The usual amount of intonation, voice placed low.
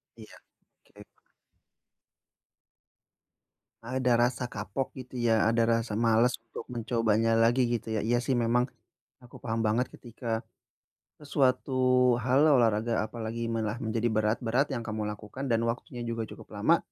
No: narrow, 1.9 semitones; low, 115 Hz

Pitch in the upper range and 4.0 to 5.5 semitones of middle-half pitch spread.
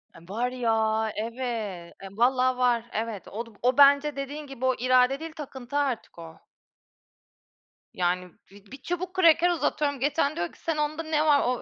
Yes: very high, 255 Hz; average, 4.6 semitones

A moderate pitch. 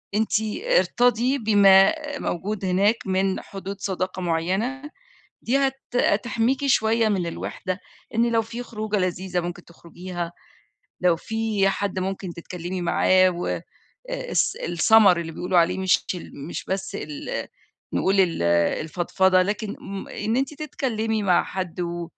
No: high, 195 Hz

